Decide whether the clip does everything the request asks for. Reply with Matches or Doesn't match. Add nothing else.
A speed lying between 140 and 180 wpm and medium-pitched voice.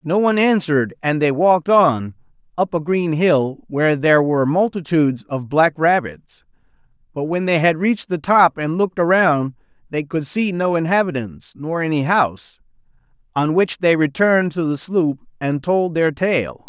Matches